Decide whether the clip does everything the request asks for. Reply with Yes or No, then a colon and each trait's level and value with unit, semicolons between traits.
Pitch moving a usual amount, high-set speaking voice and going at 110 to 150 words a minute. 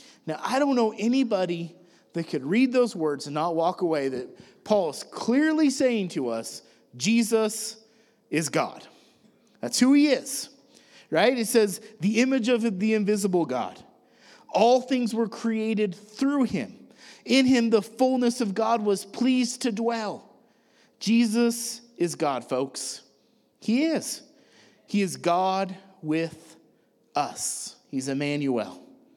No: wide, 5.7 semitones; high, 220 Hz; slow, 135 wpm